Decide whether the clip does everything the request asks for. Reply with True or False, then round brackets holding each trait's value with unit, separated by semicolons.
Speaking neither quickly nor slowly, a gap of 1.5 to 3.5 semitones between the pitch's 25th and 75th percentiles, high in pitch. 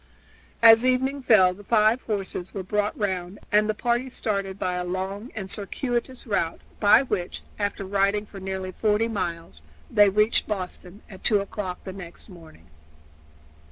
True (155 wpm; 2.6 semitones; 205 Hz)